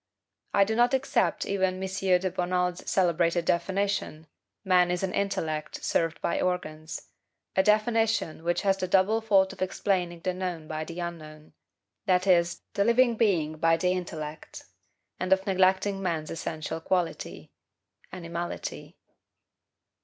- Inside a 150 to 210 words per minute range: No, average, 140 wpm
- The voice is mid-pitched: Yes, medium, 180 Hz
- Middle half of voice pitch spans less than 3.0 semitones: Yes, narrow, 2.5 semitones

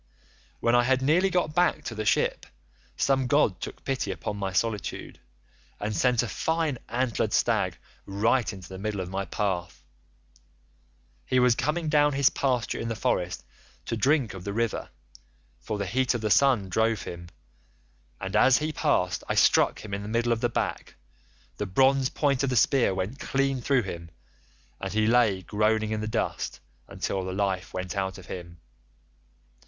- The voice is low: Yes, low, 110 Hz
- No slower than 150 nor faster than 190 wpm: Yes, average, 180 wpm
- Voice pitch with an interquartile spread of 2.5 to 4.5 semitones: No, average, 5.2 semitones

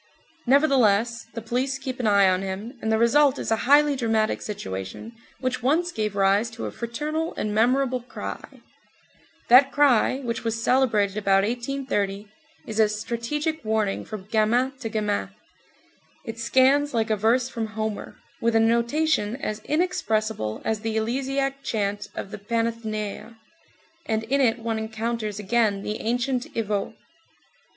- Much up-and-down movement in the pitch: No, average, 3.3 semitones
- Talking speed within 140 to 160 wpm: Yes, average, 150 wpm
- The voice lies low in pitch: No, high, 230 Hz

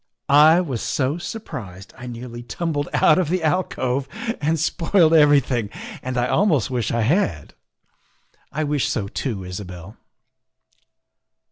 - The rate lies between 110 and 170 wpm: Yes, slow, 135 wpm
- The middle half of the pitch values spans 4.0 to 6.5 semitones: Yes, wide, 5.4 semitones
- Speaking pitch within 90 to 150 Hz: Yes, low, 135 Hz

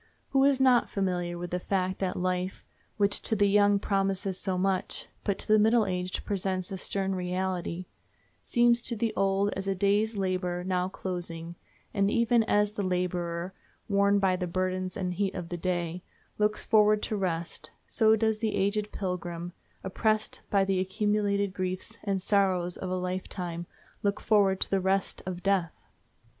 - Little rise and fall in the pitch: Yes, narrow, 2.1 semitones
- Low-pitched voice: No, high, 190 Hz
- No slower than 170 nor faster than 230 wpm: Yes, average, 175 wpm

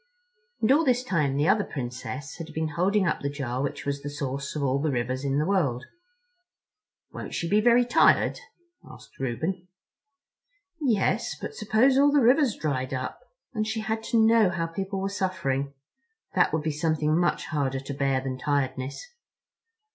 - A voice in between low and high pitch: Yes, medium, 160 Hz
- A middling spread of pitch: No, wide, 7.6 semitones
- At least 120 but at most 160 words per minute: No, average, 170 wpm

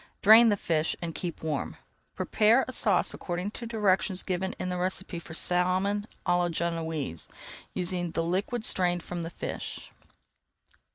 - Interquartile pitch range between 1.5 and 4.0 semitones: Yes, average, 2.8 semitones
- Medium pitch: Yes, medium, 180 Hz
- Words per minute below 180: Yes, average, 155 wpm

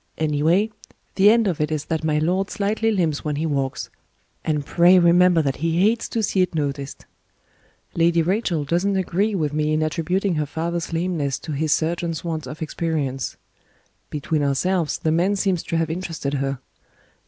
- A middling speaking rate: Yes, average, 175 wpm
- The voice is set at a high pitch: No, medium, 165 Hz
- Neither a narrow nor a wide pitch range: Yes, average, 3.2 semitones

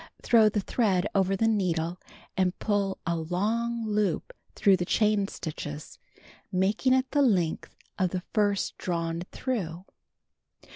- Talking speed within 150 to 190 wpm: No, slow, 135 wpm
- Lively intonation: No, average, 3.4 semitones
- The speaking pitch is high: Yes, high, 195 Hz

